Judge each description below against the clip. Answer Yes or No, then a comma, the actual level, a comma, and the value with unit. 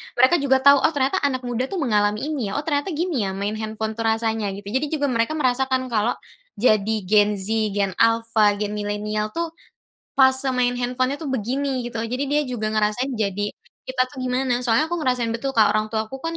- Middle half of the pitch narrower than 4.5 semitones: Yes, average, 3.7 semitones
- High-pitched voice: Yes, high, 245 Hz